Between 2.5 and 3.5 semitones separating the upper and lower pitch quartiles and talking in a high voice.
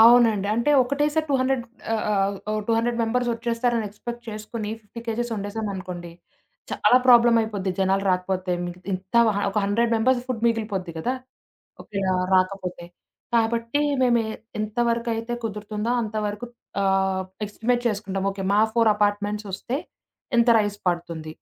Yes: average, 3.2 semitones; high, 215 Hz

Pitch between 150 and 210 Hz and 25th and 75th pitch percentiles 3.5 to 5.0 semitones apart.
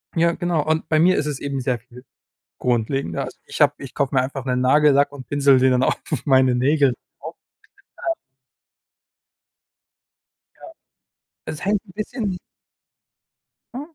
No: medium, 140 Hz; average, 3.9 semitones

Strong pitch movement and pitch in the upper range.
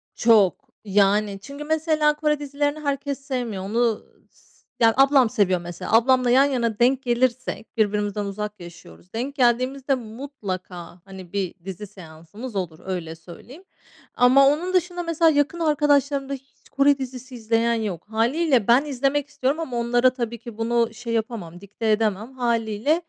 No: average, 5.0 semitones; high, 240 Hz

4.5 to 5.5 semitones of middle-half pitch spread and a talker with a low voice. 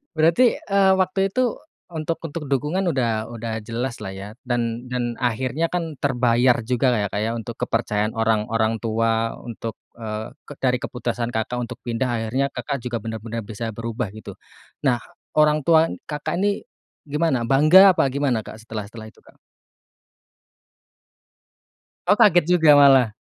Yes: average, 4.9 semitones; low, 120 Hz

